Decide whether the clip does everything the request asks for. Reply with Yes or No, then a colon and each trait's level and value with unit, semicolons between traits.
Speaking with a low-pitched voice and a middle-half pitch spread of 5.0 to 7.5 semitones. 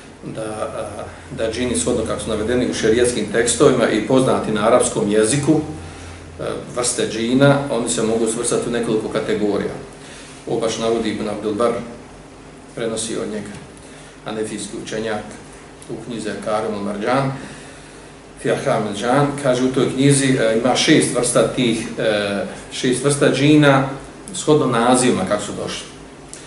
No: low, 120 Hz; average, 3.9 semitones